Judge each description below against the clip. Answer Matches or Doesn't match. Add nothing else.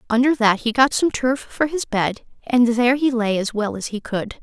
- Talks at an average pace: Doesn't match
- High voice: Matches